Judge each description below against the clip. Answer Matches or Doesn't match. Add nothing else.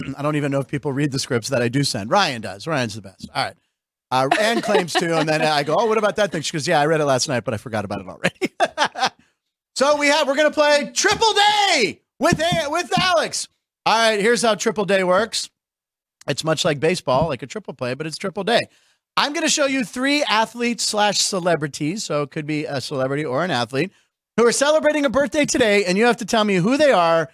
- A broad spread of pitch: Matches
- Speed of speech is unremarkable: Doesn't match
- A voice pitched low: Doesn't match